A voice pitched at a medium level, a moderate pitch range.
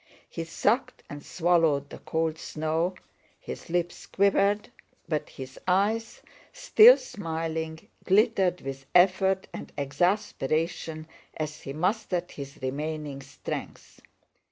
Yes: medium, 165 Hz; average, 4.0 semitones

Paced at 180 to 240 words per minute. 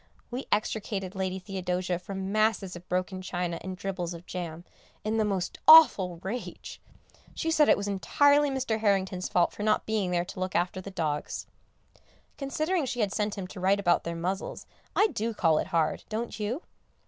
Yes: average, 185 wpm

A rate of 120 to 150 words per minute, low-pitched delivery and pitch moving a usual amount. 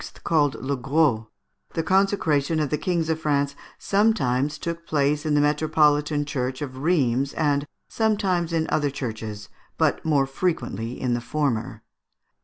No: average, 145 wpm; medium, 145 Hz; average, 3.5 semitones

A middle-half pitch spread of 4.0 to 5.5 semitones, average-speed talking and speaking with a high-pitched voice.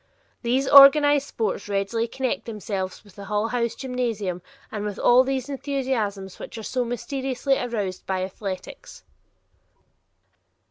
No: average, 4.6 semitones; slow, 130 wpm; high, 230 Hz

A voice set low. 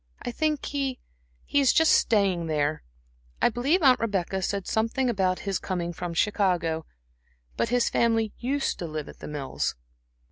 No: high, 205 Hz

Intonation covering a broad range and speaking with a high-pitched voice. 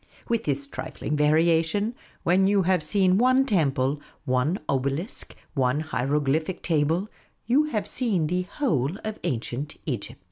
No: wide, 5.8 semitones; medium, 160 Hz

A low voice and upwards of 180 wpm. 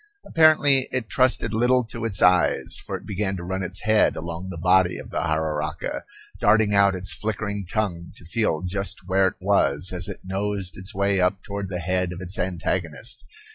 Yes: very low, 95 Hz; average, 190 wpm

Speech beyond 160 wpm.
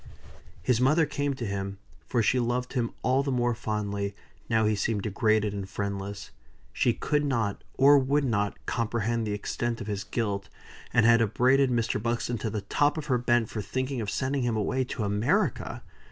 Yes: average, 185 wpm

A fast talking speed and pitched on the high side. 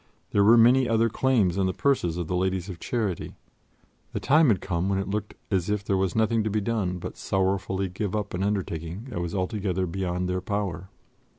No: fast, 210 wpm; very low, 95 Hz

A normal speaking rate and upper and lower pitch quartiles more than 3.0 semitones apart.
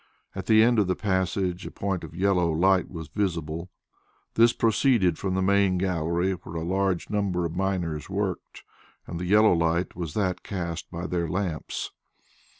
No: average, 170 wpm; narrow, 2.6 semitones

